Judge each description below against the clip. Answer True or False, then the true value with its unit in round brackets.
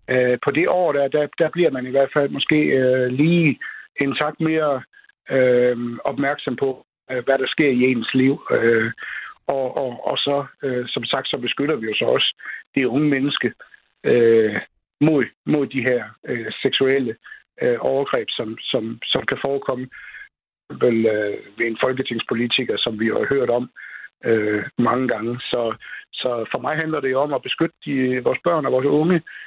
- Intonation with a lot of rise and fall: False (2.7 semitones)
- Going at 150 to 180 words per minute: True (175 wpm)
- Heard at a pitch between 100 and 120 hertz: False (130 Hz)